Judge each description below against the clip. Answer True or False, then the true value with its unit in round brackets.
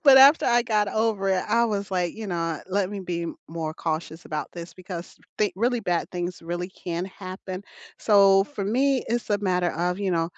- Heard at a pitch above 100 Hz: True (190 Hz)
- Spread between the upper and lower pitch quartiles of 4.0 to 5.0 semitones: False (3.4 semitones)